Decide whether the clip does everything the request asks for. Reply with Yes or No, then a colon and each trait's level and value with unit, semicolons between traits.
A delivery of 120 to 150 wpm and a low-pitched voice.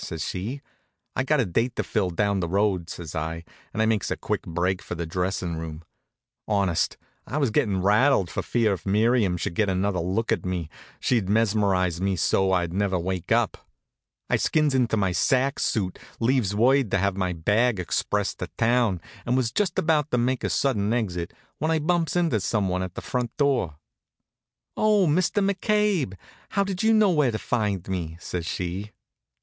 No: average, 190 wpm; low, 105 Hz